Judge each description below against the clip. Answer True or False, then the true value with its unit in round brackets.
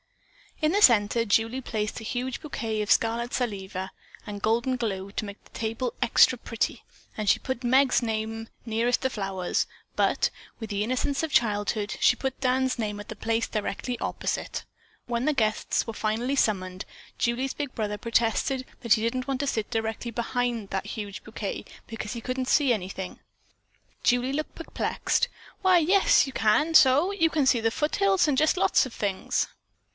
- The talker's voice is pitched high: True (235 Hz)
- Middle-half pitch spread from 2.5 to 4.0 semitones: True (3.4 semitones)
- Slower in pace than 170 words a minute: False (175 wpm)